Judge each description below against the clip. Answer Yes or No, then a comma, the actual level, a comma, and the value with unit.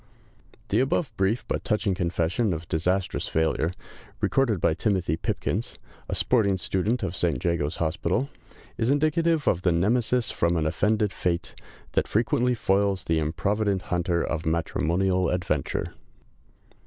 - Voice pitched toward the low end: Yes, very low, 95 Hz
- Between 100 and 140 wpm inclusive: Yes, slow, 135 wpm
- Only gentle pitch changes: No, average, 4.5 semitones